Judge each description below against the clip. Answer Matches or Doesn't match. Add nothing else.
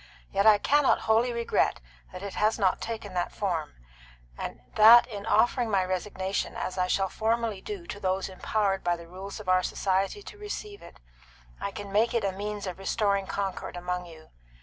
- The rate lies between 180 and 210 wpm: Matches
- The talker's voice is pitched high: Matches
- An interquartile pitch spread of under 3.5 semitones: Matches